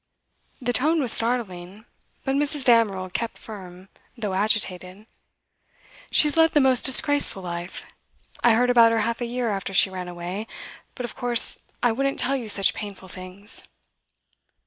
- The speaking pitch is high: Yes, high, 225 Hz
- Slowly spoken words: No, average, 160 wpm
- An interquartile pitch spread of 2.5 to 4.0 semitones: No, average, 4.7 semitones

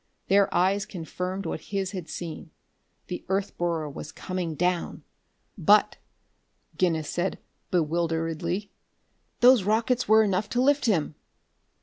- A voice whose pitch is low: No, medium, 185 Hz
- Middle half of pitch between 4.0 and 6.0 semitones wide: No, average, 3.3 semitones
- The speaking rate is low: Yes, slow, 120 wpm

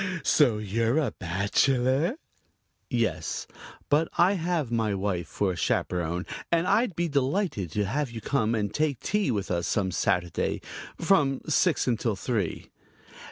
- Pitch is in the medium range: No, low, 120 Hz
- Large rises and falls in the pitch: Yes, wide, 7.6 semitones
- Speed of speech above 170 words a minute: No, average, 145 wpm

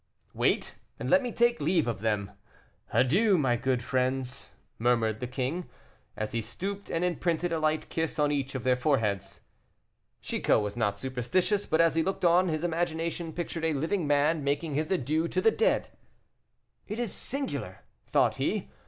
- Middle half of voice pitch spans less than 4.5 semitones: No, wide, 5.5 semitones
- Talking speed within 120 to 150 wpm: No, average, 170 wpm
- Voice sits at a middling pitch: Yes, medium, 155 Hz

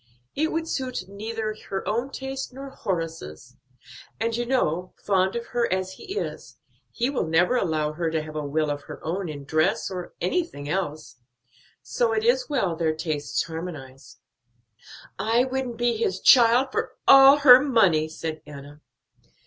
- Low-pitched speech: No, high, 190 Hz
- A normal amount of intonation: No, wide, 7.7 semitones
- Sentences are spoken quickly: No, average, 165 wpm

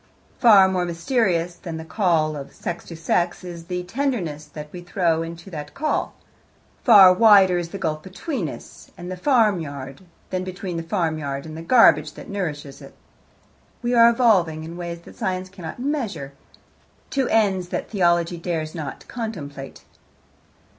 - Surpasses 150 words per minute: Yes, average, 160 wpm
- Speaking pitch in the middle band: Yes, medium, 175 Hz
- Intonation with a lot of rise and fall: No, average, 3.6 semitones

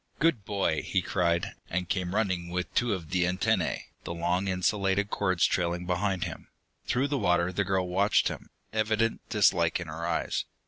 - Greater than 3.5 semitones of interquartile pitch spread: No, average, 2.7 semitones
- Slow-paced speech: No, average, 175 wpm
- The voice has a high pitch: No, very low, 90 Hz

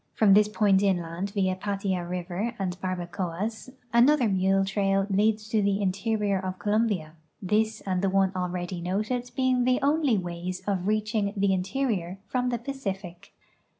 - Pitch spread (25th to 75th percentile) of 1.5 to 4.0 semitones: Yes, average, 2.8 semitones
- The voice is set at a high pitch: Yes, high, 195 Hz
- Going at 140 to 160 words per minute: Yes, average, 155 wpm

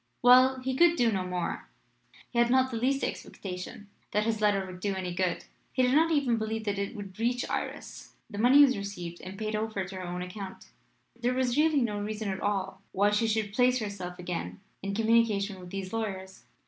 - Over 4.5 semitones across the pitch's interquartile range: No, average, 4.2 semitones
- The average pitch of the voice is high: Yes, high, 210 Hz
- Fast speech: Yes, fast, 210 wpm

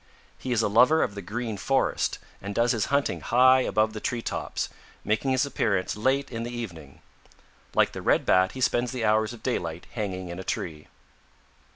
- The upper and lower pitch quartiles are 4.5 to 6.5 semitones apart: No, average, 4.1 semitones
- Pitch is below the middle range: Yes, low, 110 Hz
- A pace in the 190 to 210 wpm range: Yes, average, 195 wpm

